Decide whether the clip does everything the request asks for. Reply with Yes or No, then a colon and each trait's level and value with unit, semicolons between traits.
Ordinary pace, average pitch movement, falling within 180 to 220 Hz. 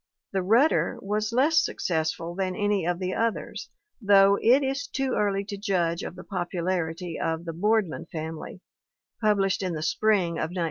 Yes: average, 170 wpm; average, 3.6 semitones; high, 190 Hz